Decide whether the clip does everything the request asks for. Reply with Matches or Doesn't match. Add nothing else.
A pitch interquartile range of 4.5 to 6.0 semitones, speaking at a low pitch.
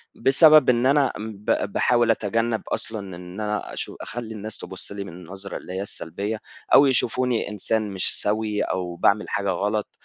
Doesn't match